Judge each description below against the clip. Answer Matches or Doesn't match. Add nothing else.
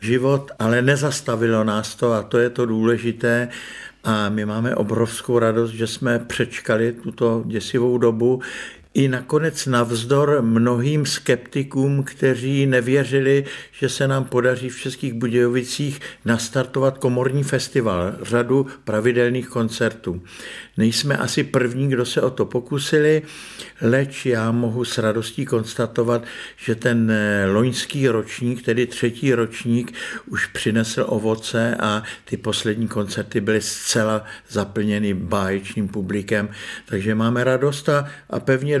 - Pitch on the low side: Matches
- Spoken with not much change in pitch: Doesn't match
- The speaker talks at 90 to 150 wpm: Matches